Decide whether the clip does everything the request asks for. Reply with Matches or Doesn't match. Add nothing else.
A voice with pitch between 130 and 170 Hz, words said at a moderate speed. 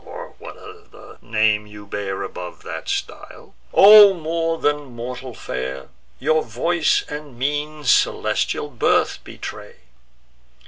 Doesn't match